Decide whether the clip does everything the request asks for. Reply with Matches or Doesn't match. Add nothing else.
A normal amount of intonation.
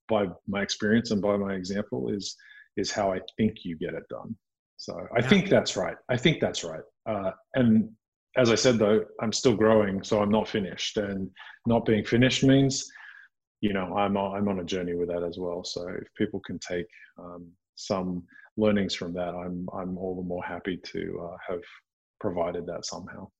Matches